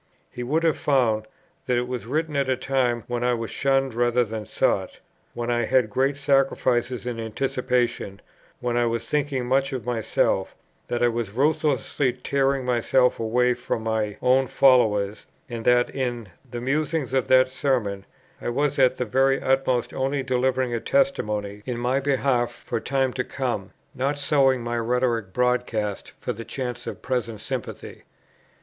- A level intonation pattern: Yes, narrow, 2.2 semitones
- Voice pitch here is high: No, low, 125 Hz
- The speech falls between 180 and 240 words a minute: No, average, 165 wpm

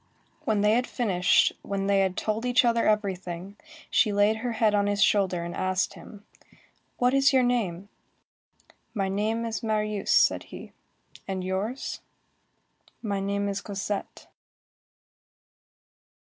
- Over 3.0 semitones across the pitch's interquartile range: No, narrow, 2.4 semitones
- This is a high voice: Yes, high, 205 Hz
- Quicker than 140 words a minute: No, slow, 135 wpm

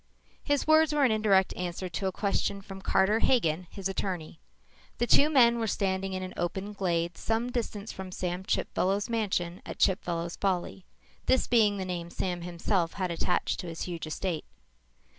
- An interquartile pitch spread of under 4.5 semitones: Yes, average, 3.3 semitones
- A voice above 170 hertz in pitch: Yes, high, 190 Hz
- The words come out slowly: No, average, 175 wpm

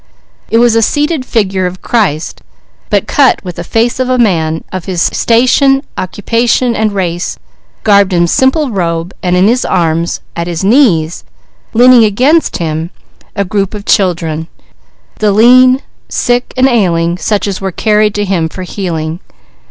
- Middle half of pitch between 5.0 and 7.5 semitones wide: Yes, wide, 5.6 semitones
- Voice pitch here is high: Yes, high, 200 Hz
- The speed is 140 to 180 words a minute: Yes, average, 160 wpm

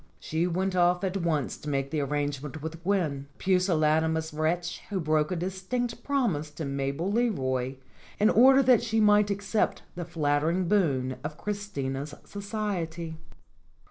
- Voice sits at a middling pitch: Yes, medium, 170 Hz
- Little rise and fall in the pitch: No, average, 5.2 semitones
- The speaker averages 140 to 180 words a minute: Yes, average, 145 wpm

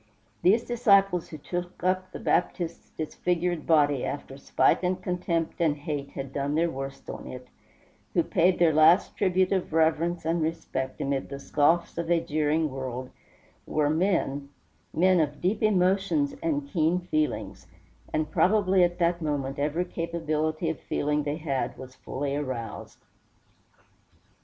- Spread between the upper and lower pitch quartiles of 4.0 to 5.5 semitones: No, average, 3.6 semitones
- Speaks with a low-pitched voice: No, medium, 165 Hz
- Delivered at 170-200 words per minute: No, average, 145 wpm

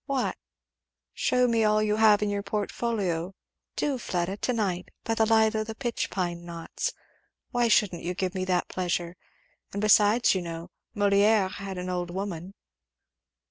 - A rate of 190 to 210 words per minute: No, average, 165 wpm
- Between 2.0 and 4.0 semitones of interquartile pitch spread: Yes, average, 3.5 semitones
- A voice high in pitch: Yes, high, 200 Hz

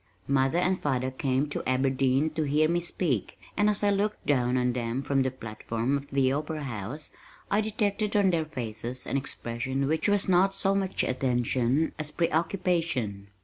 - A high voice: No, medium, 140 Hz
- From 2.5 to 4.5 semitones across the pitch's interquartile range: No, wide, 5.4 semitones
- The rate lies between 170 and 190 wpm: Yes, average, 175 wpm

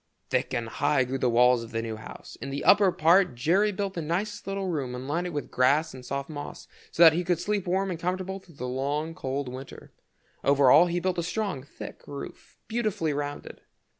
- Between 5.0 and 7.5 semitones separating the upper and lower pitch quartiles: Yes, wide, 5.6 semitones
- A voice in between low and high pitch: Yes, medium, 155 Hz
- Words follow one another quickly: Yes, fast, 220 wpm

